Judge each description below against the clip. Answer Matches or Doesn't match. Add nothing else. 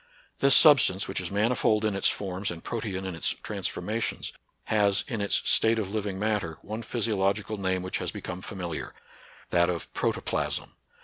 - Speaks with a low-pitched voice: Matches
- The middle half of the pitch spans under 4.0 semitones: Matches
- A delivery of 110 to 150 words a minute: Doesn't match